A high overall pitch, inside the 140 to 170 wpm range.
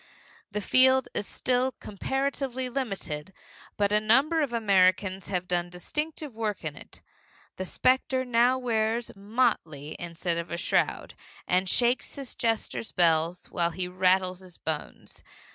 Yes: high, 210 Hz; average, 145 wpm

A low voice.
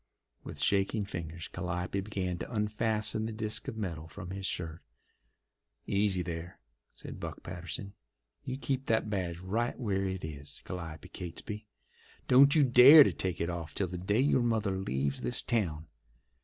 Yes: very low, 95 Hz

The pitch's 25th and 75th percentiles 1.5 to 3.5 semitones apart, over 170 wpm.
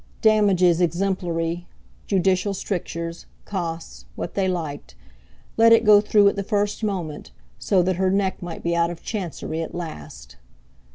No: average, 3.2 semitones; average, 145 wpm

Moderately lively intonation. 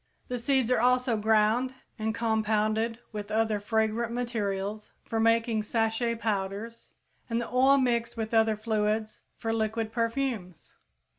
No: narrow, 1.5 semitones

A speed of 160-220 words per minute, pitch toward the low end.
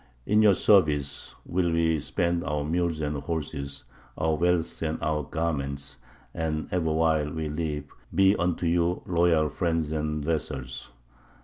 No: average, 140 wpm; very low, 80 Hz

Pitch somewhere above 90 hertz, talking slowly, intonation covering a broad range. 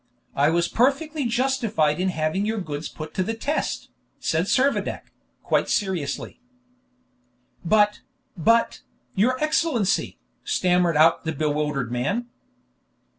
Yes: medium, 185 Hz; slow, 120 wpm; wide, 7.0 semitones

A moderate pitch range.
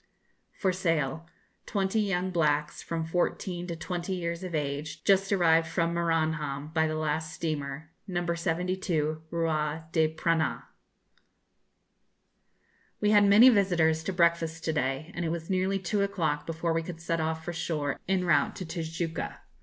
No: narrow, 2.2 semitones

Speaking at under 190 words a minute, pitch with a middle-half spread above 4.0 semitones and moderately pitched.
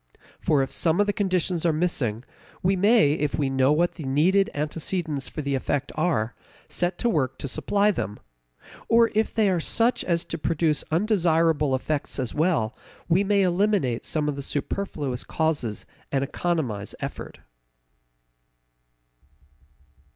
Yes: average, 150 wpm; average, 4.9 semitones; medium, 160 Hz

